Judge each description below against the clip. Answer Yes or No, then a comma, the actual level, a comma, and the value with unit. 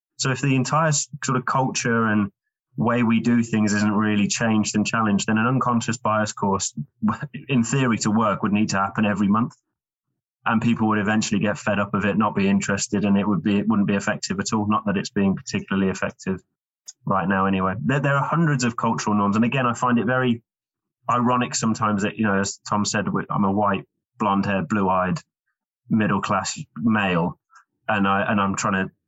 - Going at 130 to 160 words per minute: No, average, 200 wpm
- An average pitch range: Yes, average, 3.2 semitones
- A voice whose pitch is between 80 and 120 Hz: Yes, low, 110 Hz